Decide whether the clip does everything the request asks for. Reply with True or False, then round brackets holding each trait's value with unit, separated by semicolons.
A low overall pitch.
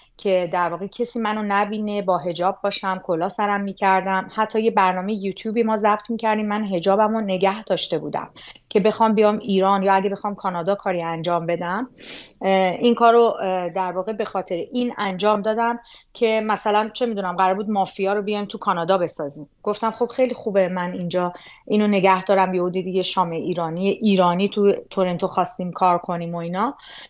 False (195 Hz)